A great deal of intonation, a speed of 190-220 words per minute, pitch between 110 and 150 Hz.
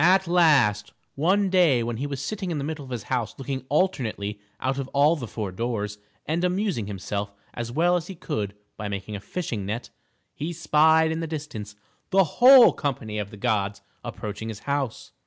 Yes: wide, 7.5 semitones; average, 195 wpm; low, 135 Hz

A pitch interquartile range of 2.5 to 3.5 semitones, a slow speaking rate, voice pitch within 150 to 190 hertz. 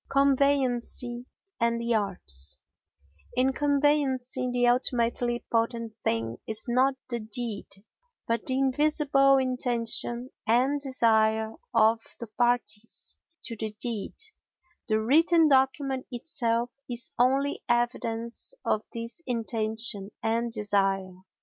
No: average, 2.8 semitones; slow, 105 wpm; high, 240 Hz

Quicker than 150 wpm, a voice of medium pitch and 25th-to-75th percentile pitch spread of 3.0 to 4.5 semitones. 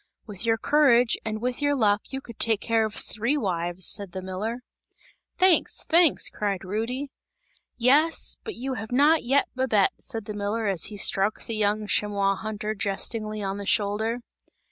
No: average, 170 wpm; high, 220 Hz; average, 3.6 semitones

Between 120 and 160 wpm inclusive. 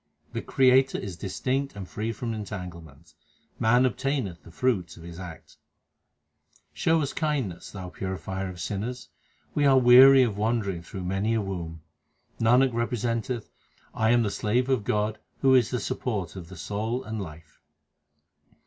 Yes: average, 155 wpm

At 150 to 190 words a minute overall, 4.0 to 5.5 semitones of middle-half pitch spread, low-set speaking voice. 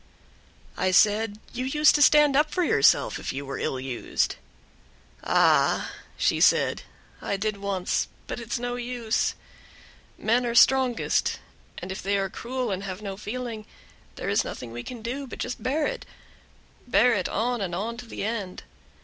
No: average, 175 wpm; average, 4.3 semitones; high, 225 Hz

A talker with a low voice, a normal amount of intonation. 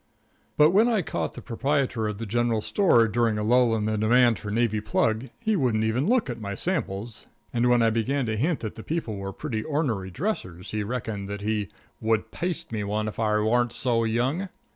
Yes: low, 115 Hz; average, 3.5 semitones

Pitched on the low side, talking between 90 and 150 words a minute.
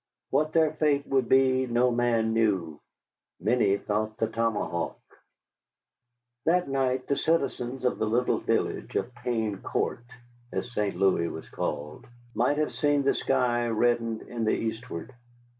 Yes: low, 120 Hz; average, 140 wpm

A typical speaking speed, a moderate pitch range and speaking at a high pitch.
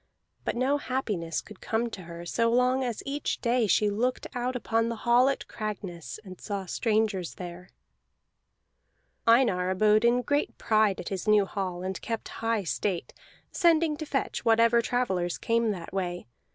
Yes: average, 165 wpm; average, 4.4 semitones; high, 220 Hz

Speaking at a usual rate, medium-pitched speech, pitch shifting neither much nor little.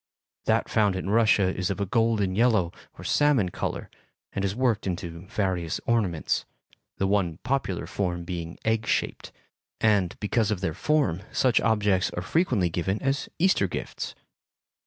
No: average, 155 wpm; low, 100 Hz; average, 3.9 semitones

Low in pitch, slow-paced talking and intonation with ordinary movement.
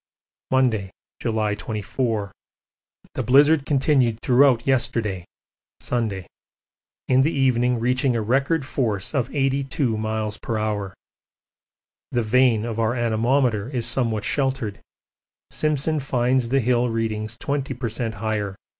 Yes: low, 120 Hz; slow, 115 wpm; average, 3.3 semitones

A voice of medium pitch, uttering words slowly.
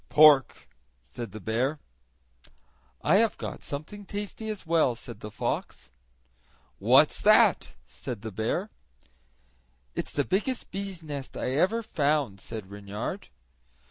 Yes: medium, 145 Hz; slow, 125 wpm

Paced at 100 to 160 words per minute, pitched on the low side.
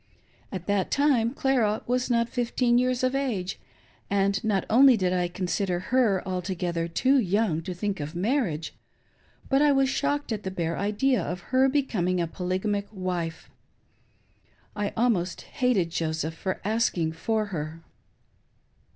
No: average, 150 wpm; high, 200 Hz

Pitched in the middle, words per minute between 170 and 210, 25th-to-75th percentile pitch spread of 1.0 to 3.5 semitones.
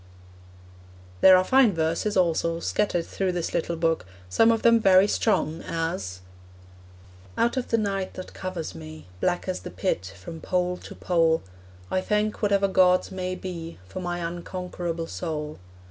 No: medium, 180 Hz; average, 155 wpm; average, 2.7 semitones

